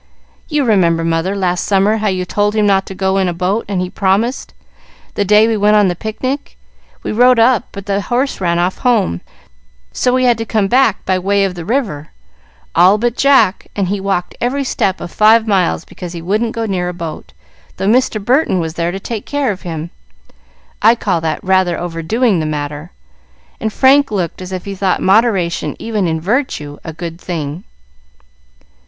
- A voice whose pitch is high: Yes, high, 195 Hz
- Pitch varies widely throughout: No, average, 4.2 semitones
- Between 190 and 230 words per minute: Yes, average, 195 wpm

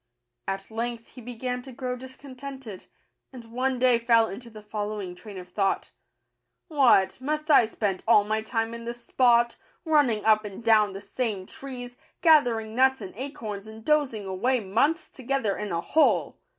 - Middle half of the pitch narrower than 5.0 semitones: Yes, average, 3.5 semitones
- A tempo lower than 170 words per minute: No, average, 175 wpm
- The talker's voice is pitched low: No, high, 235 Hz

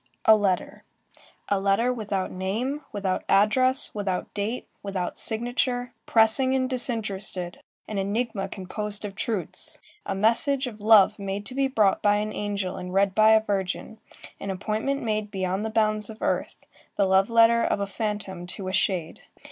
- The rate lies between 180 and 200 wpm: No, average, 165 wpm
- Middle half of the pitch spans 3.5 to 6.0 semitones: No, average, 2.7 semitones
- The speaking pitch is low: No, high, 210 Hz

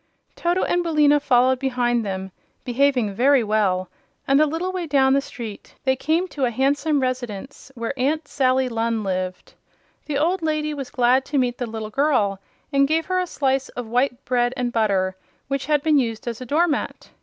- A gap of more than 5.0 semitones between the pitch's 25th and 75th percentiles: No, average, 3.9 semitones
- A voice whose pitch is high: Yes, very high, 260 Hz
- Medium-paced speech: Yes, average, 190 wpm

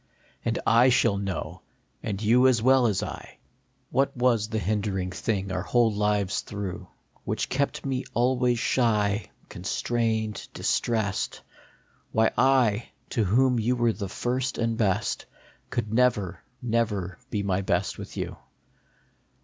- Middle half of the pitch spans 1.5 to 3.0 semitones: No, average, 3.4 semitones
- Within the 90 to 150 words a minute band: Yes, average, 140 wpm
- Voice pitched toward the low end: Yes, low, 110 Hz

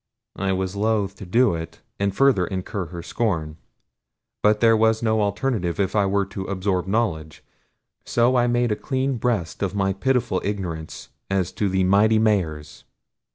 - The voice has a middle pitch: No, low, 100 Hz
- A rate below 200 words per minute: Yes, average, 165 wpm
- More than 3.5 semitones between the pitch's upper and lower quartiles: No, average, 3.1 semitones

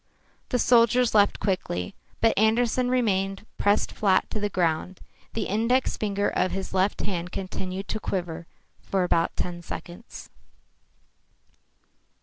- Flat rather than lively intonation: No, average, 3.4 semitones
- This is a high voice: Yes, high, 195 Hz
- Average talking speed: No, slow, 130 wpm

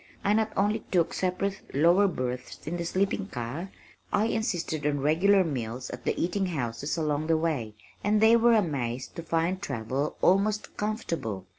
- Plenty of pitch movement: Yes, wide, 6.3 semitones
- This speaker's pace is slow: No, average, 165 wpm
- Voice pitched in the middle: Yes, medium, 170 Hz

